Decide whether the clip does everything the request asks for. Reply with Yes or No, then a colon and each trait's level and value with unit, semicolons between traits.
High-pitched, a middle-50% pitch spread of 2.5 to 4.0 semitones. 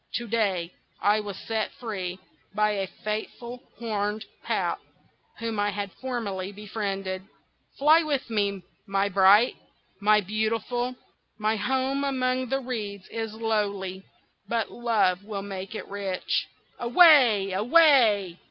Yes: high, 215 Hz; average, 3.2 semitones